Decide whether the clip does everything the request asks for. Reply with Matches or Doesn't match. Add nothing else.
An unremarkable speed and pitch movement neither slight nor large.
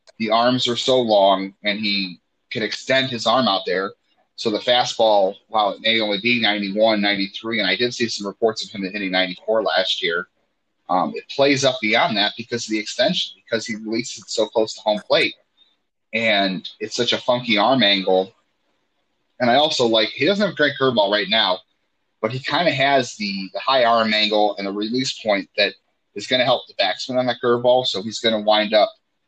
Doesn't match